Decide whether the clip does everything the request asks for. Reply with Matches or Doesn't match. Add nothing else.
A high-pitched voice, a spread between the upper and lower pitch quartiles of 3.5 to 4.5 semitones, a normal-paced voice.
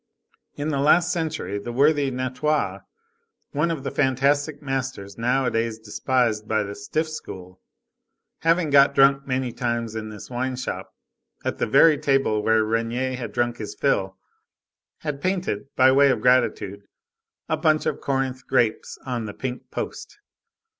Doesn't match